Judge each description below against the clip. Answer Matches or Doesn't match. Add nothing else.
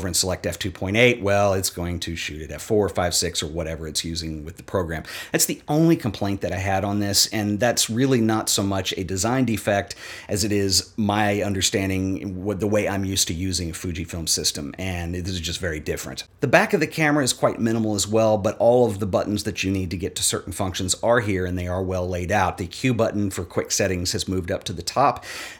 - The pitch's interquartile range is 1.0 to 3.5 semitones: Matches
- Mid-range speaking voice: Doesn't match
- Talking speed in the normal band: Doesn't match